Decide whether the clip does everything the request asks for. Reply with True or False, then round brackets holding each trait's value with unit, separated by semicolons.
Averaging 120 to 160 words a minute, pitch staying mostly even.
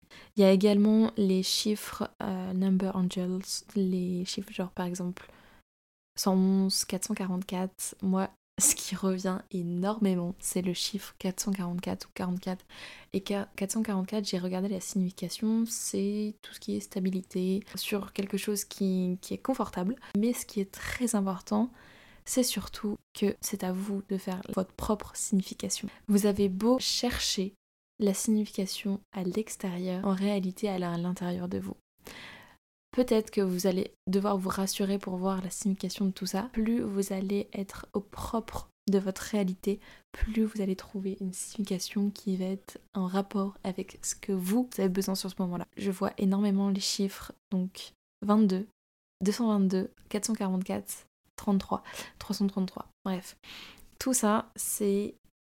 True (150 wpm; 1.7 semitones)